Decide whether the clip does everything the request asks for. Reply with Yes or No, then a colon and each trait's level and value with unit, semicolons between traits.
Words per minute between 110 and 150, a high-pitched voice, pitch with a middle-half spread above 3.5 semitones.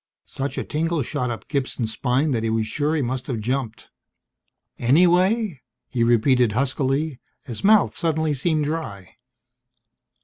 No: average, 140 wpm; low, 135 Hz; average, 4.8 semitones